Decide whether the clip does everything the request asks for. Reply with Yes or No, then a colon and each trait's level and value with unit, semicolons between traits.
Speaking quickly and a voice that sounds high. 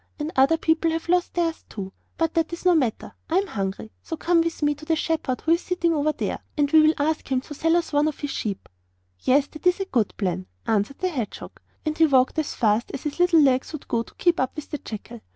Yes: fast, 255 wpm; very high, 305 Hz